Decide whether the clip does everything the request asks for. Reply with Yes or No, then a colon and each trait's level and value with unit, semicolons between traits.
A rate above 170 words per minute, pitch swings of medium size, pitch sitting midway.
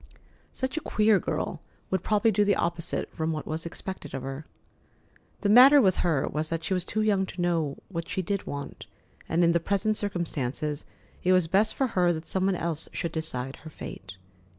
Yes: average, 200 wpm; average, 4.0 semitones; medium, 175 Hz